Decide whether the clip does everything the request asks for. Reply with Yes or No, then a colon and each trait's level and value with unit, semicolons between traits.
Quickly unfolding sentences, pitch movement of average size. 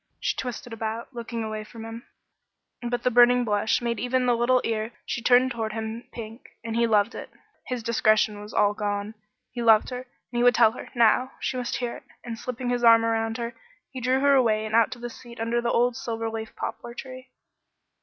No: fast, 220 wpm; narrow, 1.7 semitones